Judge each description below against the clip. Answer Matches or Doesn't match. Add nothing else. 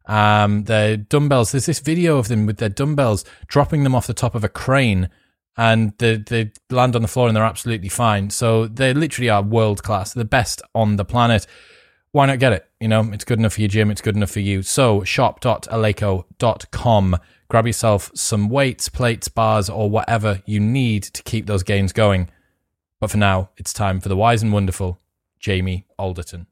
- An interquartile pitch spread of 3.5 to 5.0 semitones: Doesn't match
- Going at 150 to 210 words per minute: Matches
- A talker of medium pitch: Doesn't match